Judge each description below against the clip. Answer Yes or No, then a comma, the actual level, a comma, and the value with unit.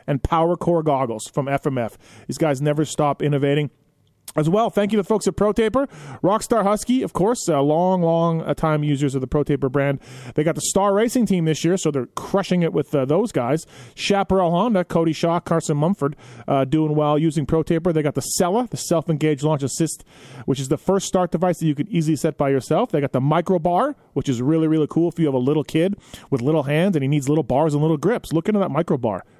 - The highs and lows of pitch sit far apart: No, average, 3.6 semitones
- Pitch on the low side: No, medium, 155 Hz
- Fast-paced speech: Yes, fast, 225 wpm